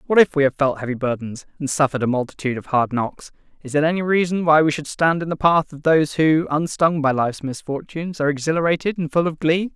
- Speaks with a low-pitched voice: No, medium, 150 Hz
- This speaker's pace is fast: Yes, fast, 235 wpm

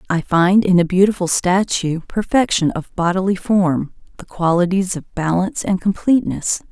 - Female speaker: Yes, female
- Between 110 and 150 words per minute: Yes, average, 145 wpm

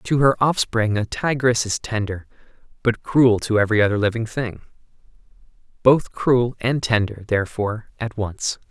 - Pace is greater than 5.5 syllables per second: No, 4.8 syllables/s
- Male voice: Yes, male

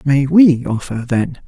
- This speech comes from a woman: No, male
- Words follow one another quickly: No, average, 165 wpm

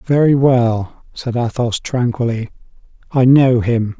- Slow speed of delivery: Yes, slow, 120 wpm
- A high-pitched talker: No, low, 120 Hz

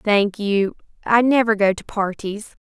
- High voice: Yes, high, 210 Hz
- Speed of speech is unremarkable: Yes, average, 160 wpm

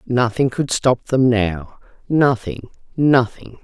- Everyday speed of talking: No, slow, 115 wpm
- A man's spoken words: No, female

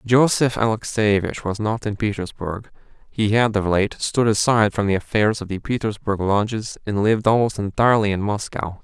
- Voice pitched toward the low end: Yes, low, 105 Hz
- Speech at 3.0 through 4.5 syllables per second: No, 5.2 syllables/s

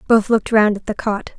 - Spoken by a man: No, female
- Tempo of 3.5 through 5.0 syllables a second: No, 5.9 syllables/s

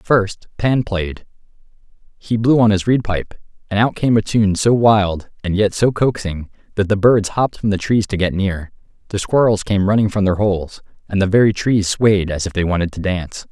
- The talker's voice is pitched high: No, low, 100 Hz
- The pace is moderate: No, fast, 215 wpm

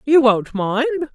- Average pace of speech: Yes, average, 155 wpm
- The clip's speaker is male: No, female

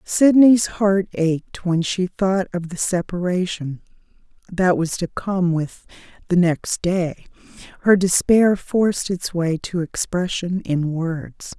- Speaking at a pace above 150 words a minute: No, slow, 135 wpm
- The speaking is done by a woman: Yes, female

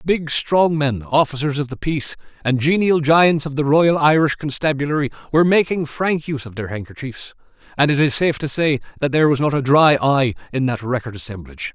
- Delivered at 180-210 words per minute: Yes, average, 200 wpm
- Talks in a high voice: No, medium, 140 Hz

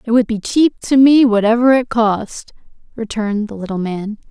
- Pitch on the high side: Yes, high, 225 Hz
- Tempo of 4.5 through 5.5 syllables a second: Yes, 5.0 syllables/s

